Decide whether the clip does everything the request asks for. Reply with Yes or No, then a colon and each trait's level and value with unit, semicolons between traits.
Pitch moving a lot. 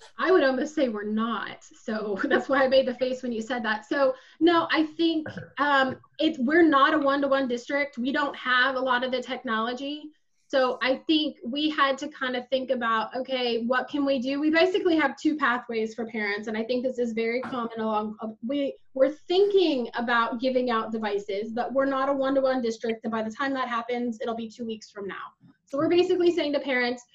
No: average, 3.4 semitones